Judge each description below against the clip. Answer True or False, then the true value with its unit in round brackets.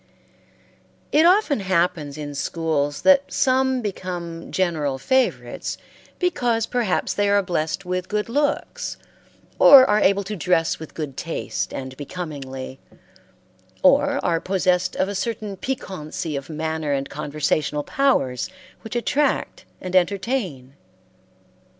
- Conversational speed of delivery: False (120 wpm)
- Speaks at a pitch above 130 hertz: True (185 Hz)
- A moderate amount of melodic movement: False (7.2 semitones)